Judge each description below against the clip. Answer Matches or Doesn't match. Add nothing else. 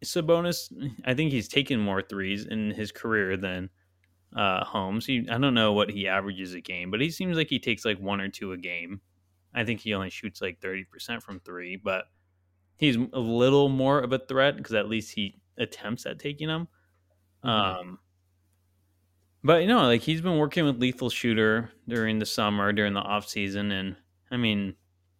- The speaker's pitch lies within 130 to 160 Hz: Doesn't match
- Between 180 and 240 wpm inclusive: Matches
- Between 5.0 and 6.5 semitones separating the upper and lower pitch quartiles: Matches